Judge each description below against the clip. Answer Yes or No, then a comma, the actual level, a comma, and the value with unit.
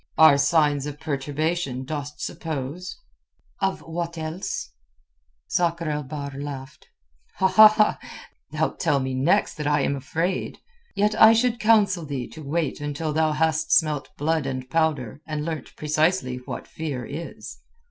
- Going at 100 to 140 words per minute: Yes, slow, 135 wpm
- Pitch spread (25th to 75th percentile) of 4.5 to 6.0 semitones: No, average, 3.2 semitones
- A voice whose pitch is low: No, medium, 155 Hz